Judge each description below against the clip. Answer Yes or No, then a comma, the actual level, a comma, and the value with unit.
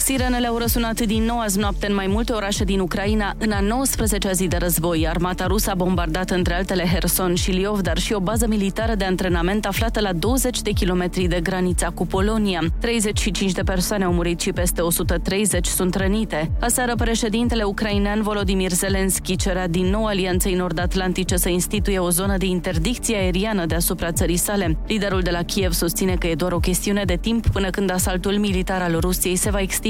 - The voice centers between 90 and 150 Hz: No, high, 195 Hz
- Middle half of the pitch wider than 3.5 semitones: No, average, 2.7 semitones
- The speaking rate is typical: No, fast, 190 wpm